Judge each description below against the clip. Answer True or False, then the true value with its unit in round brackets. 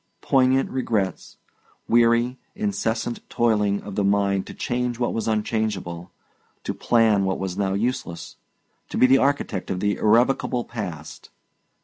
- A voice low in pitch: True (110 Hz)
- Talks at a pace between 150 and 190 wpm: False (135 wpm)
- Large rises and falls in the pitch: False (3.6 semitones)